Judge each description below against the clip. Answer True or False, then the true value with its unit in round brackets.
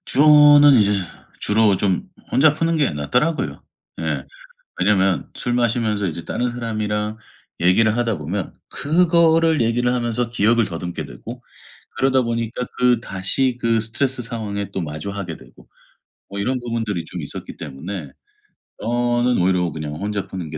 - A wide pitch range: False (4.4 semitones)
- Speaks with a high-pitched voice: False (115 Hz)